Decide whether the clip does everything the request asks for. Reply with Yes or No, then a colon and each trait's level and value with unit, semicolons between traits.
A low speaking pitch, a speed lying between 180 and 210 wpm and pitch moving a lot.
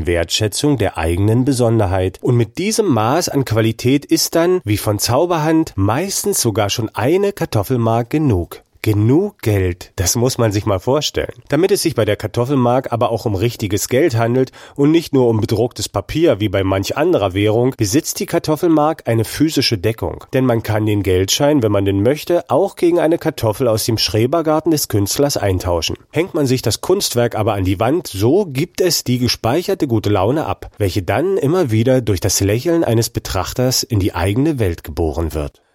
Yes: low, 115 Hz; average, 185 wpm; wide, 5.8 semitones